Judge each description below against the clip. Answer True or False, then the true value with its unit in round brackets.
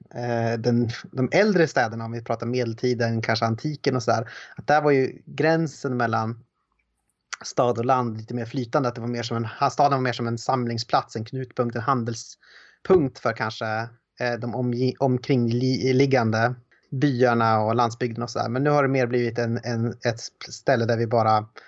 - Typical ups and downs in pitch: False (2.3 semitones)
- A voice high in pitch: False (120 Hz)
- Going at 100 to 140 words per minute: False (175 wpm)